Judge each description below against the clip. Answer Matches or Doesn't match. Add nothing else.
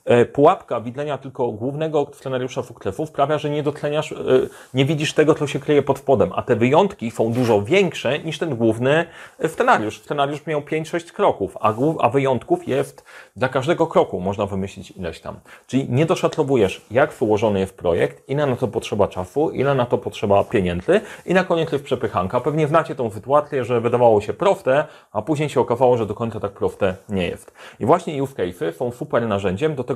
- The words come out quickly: Matches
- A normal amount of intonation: Matches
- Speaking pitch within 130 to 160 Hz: Matches